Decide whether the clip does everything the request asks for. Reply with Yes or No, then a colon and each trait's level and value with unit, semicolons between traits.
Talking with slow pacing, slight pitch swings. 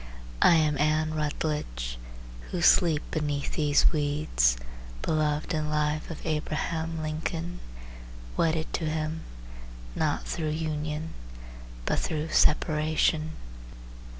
Yes: slow, 100 wpm; narrow, 1.0 semitones